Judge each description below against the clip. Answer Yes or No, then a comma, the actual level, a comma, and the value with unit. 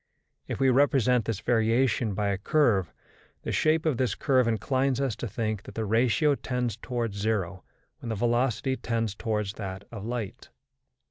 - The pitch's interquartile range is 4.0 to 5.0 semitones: No, average, 3.3 semitones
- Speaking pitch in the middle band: No, low, 115 Hz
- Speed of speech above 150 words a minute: Yes, average, 170 wpm